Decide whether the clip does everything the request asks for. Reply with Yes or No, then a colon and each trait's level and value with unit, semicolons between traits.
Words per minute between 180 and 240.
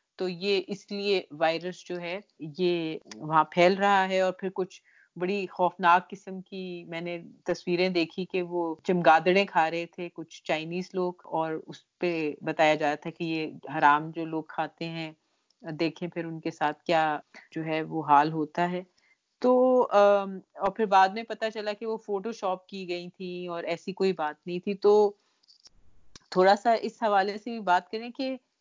Yes: average, 185 wpm